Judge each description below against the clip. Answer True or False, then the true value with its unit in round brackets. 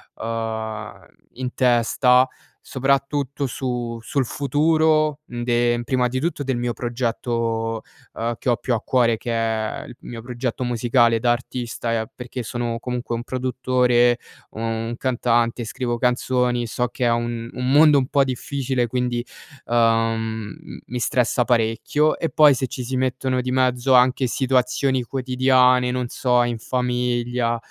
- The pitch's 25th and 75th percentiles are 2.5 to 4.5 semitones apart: False (1.7 semitones)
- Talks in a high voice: False (125 Hz)